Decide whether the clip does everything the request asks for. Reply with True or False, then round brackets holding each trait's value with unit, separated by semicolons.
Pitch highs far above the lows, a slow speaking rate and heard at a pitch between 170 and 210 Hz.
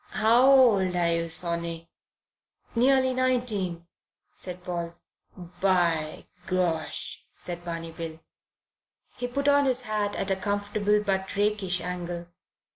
False (4.1 semitones; 120 wpm; 185 Hz)